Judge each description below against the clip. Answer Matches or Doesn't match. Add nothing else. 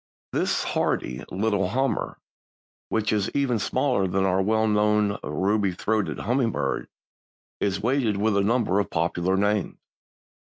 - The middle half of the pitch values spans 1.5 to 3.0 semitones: Matches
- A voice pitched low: Matches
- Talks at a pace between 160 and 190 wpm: Doesn't match